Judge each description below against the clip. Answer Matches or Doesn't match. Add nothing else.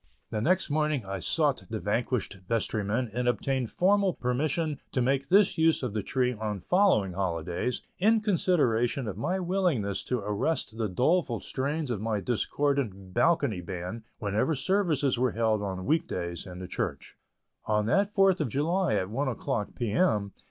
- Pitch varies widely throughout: Matches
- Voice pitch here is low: Matches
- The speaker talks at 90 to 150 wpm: Doesn't match